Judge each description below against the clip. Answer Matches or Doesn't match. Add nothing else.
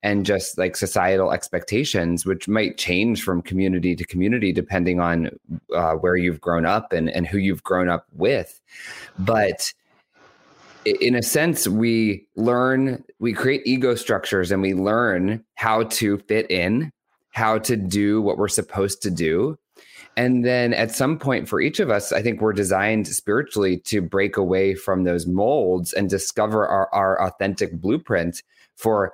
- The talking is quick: Doesn't match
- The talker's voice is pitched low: Matches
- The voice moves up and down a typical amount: Matches